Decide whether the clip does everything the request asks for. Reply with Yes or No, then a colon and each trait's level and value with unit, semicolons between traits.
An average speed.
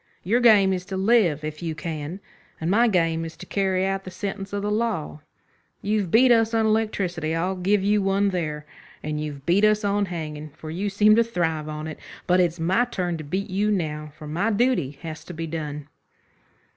No: fast, 210 wpm